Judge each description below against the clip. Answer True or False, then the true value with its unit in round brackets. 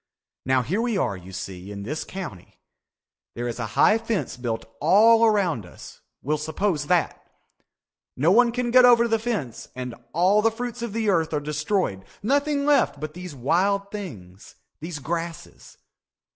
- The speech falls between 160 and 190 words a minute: True (165 wpm)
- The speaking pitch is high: False (175 Hz)